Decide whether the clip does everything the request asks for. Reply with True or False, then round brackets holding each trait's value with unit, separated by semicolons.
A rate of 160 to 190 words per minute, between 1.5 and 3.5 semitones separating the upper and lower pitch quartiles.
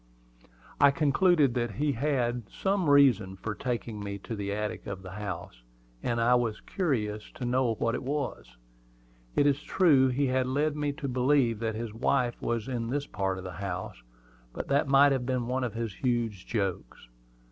False (185 wpm; 4.7 semitones)